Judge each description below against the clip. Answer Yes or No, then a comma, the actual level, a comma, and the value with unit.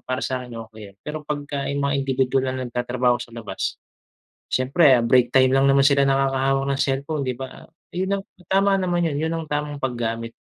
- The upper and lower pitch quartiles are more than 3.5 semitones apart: No, narrow, 2.5 semitones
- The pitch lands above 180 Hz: No, low, 135 Hz